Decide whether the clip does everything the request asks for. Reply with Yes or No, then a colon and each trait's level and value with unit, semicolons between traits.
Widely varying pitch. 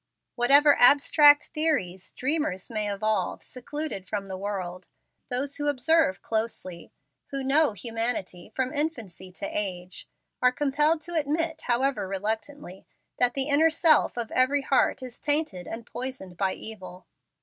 Yes: wide, 6.8 semitones